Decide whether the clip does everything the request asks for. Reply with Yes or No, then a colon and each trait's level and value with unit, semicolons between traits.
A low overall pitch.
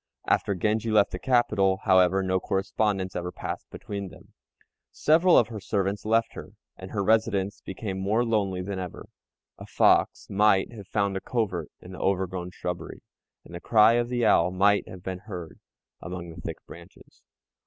Yes: very low, 95 Hz